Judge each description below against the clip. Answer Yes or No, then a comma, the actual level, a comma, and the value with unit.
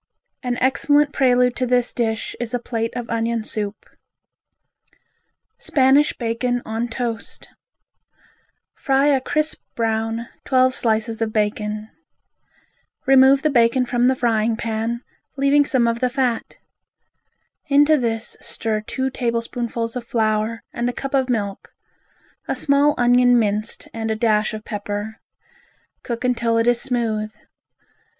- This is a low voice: No, high, 235 Hz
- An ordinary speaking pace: No, slow, 130 wpm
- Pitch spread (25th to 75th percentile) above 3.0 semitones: No, narrow, 2.5 semitones